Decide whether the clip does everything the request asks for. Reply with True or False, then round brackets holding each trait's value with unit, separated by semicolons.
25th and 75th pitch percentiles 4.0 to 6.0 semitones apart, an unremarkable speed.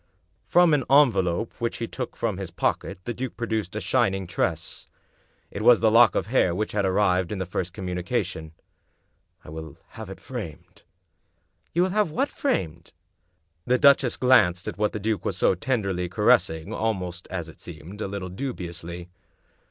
True (5.0 semitones; 175 wpm)